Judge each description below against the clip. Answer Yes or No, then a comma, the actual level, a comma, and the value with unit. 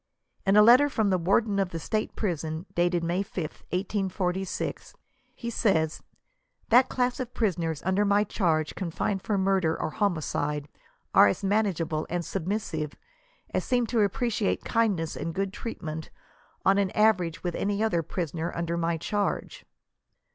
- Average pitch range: Yes, average, 4.0 semitones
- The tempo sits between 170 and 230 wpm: No, average, 155 wpm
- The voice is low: No, high, 190 Hz